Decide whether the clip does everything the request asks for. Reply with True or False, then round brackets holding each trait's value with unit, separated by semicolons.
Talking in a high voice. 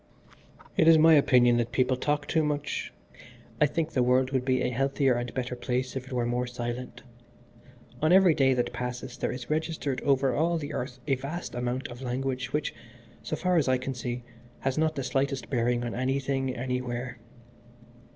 False (130 Hz)